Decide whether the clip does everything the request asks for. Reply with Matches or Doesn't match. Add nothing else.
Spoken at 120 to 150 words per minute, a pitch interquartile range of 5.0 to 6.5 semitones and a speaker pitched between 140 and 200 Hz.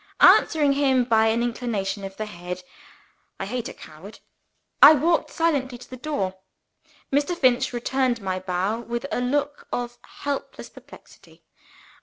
Doesn't match